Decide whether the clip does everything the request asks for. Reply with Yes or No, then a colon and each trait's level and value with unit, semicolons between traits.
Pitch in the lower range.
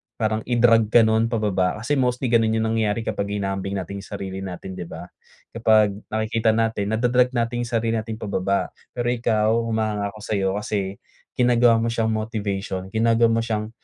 Yes: low, 110 Hz